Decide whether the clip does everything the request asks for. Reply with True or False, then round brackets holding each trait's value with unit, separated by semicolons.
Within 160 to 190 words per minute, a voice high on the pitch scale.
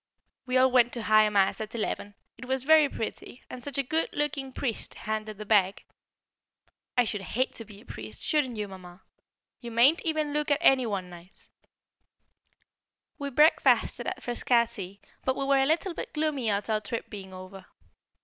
True (180 wpm; 235 Hz)